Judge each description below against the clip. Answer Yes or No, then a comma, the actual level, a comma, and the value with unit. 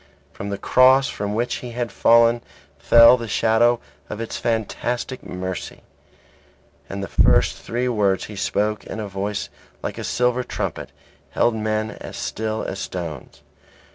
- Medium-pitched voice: No, low, 110 Hz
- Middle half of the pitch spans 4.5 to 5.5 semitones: No, average, 3.0 semitones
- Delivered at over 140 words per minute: Yes, average, 150 wpm